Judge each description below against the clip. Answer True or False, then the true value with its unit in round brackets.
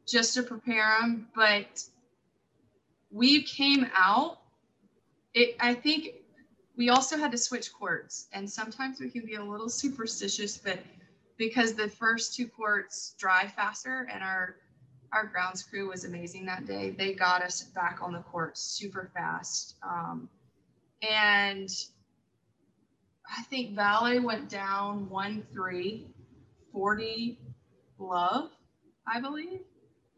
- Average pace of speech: False (125 wpm)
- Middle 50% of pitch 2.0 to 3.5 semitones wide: False (4.3 semitones)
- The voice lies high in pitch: True (210 Hz)